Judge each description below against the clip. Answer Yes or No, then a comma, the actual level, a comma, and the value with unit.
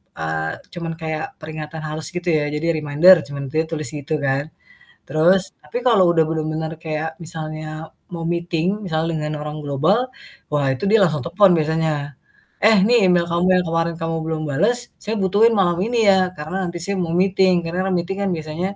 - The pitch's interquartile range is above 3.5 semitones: No, average, 2.9 semitones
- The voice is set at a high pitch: No, medium, 165 Hz